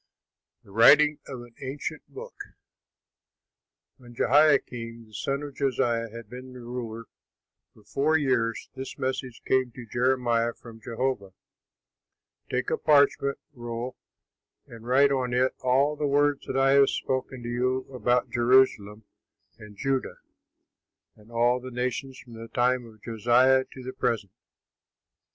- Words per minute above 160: No, slow, 135 wpm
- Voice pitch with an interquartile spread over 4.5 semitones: No, narrow, 2.4 semitones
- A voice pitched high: No, low, 125 Hz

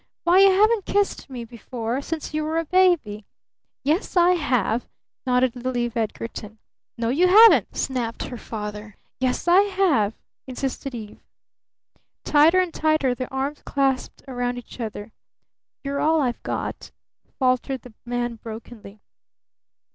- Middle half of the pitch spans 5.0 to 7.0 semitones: Yes, wide, 5.4 semitones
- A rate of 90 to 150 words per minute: Yes, average, 140 wpm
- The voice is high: Yes, very high, 255 Hz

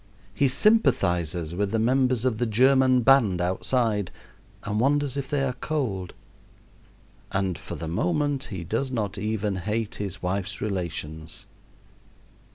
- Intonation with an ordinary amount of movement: No, wide, 5.9 semitones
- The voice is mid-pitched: No, low, 110 Hz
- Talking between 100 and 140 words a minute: Yes, slow, 135 wpm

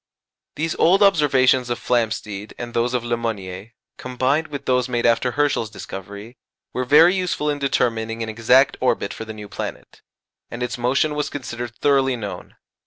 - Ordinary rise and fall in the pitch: Yes, average, 3.6 semitones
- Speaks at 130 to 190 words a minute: Yes, average, 170 wpm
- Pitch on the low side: Yes, low, 125 Hz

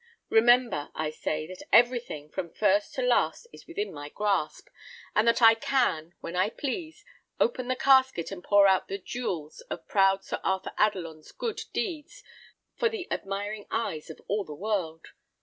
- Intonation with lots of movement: Yes, wide, 6.3 semitones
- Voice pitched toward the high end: Yes, high, 205 Hz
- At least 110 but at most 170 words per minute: Yes, average, 165 wpm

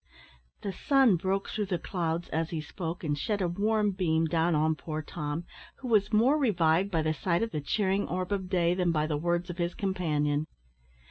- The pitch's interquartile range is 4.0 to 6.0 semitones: No, average, 3.6 semitones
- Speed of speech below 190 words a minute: No, fast, 205 wpm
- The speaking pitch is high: No, medium, 175 Hz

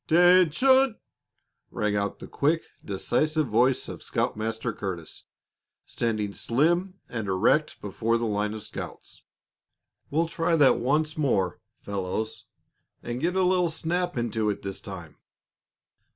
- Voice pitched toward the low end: Yes, low, 120 Hz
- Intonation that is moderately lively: No, wide, 7.7 semitones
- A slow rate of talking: Yes, slow, 125 wpm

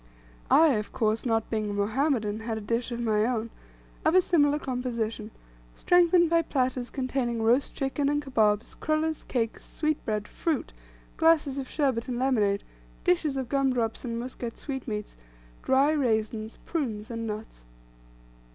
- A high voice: Yes, very high, 250 Hz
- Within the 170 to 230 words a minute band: No, average, 150 wpm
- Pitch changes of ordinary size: Yes, average, 4.5 semitones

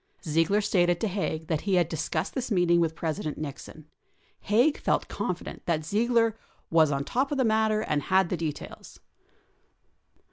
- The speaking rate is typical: Yes, average, 170 wpm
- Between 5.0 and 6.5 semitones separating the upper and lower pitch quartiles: Yes, wide, 5.4 semitones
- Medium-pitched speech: Yes, medium, 175 Hz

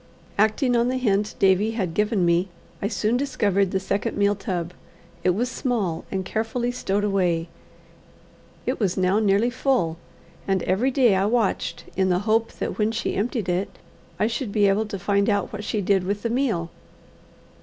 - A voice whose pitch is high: Yes, high, 205 Hz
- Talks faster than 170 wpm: Yes, average, 180 wpm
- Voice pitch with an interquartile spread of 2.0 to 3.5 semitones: Yes, average, 3.1 semitones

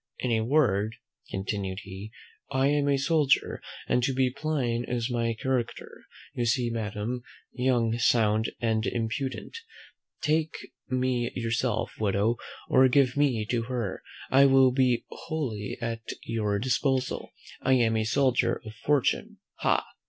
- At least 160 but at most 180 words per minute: No, average, 140 wpm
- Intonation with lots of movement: No, average, 3.0 semitones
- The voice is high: No, low, 120 Hz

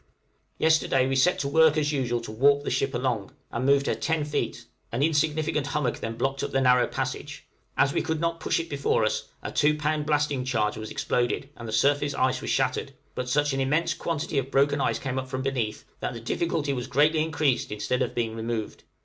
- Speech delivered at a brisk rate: Yes, fast, 220 wpm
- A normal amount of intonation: Yes, average, 3.0 semitones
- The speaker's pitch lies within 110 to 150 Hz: Yes, low, 135 Hz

